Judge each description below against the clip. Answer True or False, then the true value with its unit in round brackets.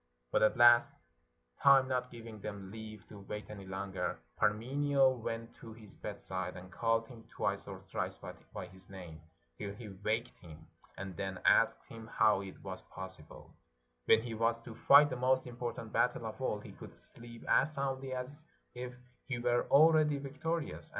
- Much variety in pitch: False (4.4 semitones)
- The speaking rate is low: False (175 wpm)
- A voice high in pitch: False (115 Hz)